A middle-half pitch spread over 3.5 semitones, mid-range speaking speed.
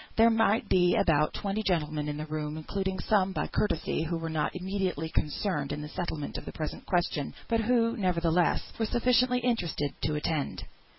Yes: wide, 5.4 semitones; average, 180 wpm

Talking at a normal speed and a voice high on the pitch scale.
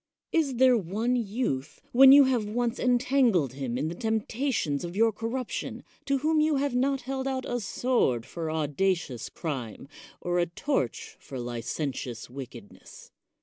Yes: average, 155 wpm; high, 225 Hz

